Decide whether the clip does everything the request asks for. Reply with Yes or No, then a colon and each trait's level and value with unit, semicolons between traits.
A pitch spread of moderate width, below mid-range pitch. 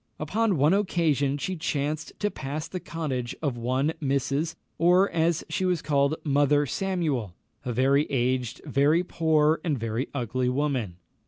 No: average, 3.8 semitones; medium, 145 Hz